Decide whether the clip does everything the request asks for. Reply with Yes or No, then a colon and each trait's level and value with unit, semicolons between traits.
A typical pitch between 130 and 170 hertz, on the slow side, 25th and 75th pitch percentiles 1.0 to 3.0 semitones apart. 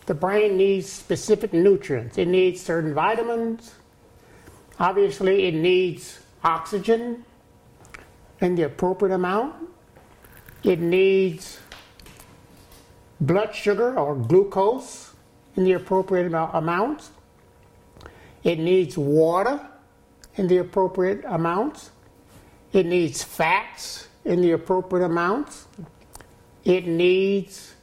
No: medium, 185 Hz; slow, 95 wpm; narrow, 2.4 semitones